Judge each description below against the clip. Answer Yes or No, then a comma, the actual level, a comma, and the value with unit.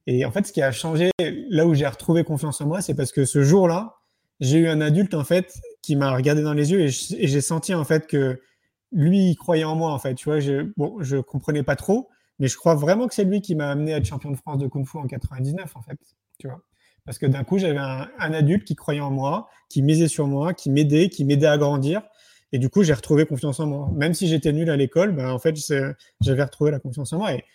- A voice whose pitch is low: No, medium, 150 Hz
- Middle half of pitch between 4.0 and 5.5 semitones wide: No, average, 3.2 semitones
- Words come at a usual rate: No, fast, 270 wpm